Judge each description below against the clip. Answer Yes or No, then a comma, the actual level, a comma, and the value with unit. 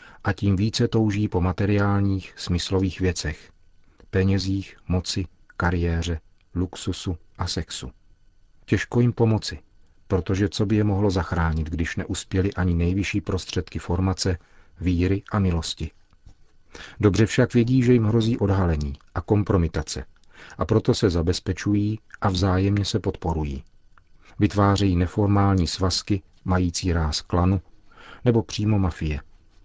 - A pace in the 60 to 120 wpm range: Yes, slow, 115 wpm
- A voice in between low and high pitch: No, very low, 95 Hz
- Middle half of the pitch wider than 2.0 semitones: Yes, average, 2.9 semitones